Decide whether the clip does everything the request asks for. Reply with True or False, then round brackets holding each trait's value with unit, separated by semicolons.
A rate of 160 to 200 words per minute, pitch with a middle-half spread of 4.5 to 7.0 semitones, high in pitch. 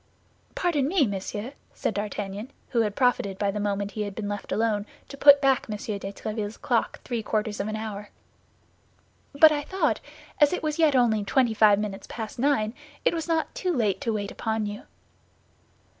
True (190 wpm; 4.9 semitones; 220 Hz)